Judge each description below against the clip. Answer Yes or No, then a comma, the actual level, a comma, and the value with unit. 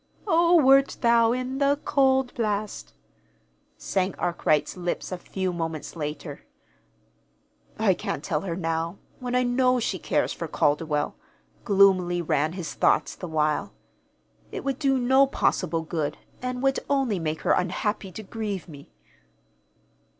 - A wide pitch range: Yes, wide, 7.4 semitones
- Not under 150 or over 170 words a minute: No, average, 140 wpm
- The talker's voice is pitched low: No, high, 200 Hz